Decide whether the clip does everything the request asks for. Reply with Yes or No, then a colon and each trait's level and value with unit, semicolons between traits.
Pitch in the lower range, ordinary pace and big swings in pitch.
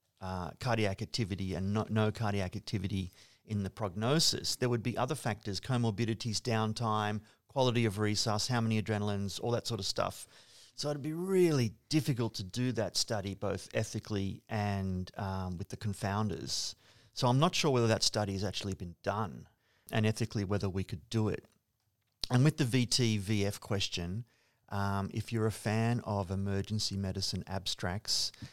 No: low, 110 Hz; average, 165 wpm; average, 2.9 semitones